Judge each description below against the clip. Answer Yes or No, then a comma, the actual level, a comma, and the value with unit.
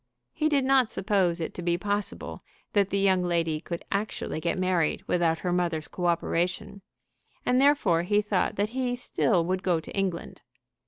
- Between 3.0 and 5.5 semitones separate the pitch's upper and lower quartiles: Yes, average, 3.3 semitones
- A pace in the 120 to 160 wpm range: No, average, 175 wpm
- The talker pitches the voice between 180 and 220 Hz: Yes, medium, 185 Hz